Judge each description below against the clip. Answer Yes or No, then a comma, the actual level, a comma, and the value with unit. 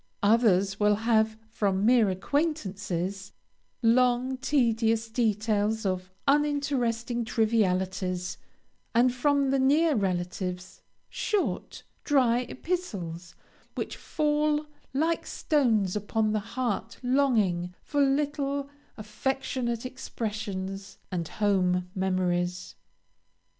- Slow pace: Yes, slow, 90 wpm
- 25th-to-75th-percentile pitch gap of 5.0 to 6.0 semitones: Yes, wide, 5.6 semitones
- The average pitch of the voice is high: Yes, high, 225 Hz